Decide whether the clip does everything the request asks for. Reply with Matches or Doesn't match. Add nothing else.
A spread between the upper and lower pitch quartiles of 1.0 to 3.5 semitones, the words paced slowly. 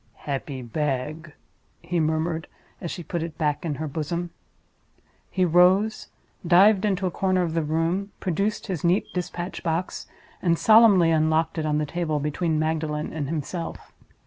Doesn't match